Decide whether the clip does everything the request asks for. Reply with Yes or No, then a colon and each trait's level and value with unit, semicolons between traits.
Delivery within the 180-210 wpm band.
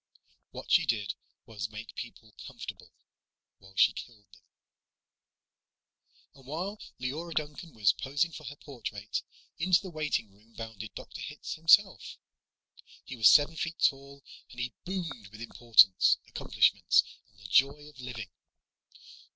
No: slow, 135 wpm